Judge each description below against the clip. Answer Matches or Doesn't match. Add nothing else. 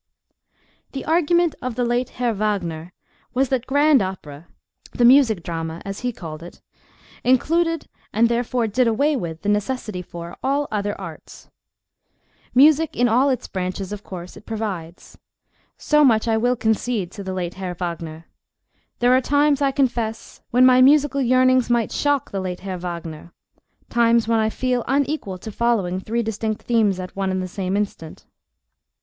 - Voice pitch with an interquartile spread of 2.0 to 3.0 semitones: Doesn't match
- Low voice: Doesn't match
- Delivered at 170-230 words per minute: Doesn't match